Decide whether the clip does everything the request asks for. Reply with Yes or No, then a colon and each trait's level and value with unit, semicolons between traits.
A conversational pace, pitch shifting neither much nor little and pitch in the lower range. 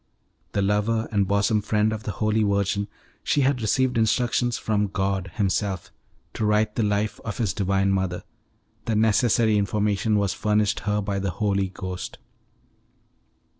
No: average, 150 wpm; narrow, 1.8 semitones; low, 105 Hz